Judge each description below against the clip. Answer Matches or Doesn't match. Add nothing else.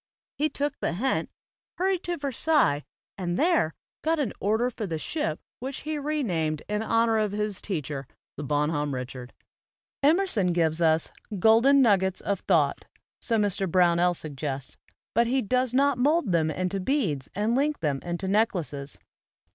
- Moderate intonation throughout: Doesn't match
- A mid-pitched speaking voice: Doesn't match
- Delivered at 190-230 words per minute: Doesn't match